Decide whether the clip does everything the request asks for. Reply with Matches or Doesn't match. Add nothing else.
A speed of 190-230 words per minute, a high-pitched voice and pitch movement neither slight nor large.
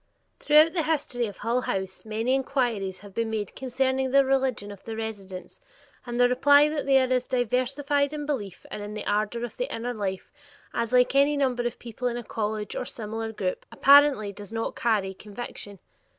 Matches